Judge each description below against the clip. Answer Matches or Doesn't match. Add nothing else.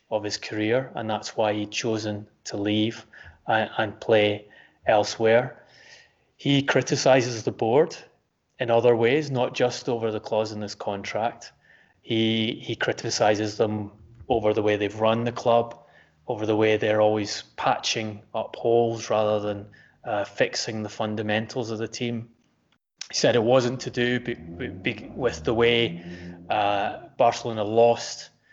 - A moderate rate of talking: Matches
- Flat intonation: Matches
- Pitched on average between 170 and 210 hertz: Doesn't match